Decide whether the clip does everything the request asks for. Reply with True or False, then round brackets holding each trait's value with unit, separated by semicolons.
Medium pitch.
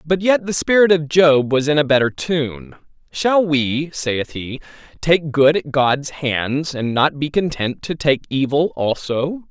True (145 Hz)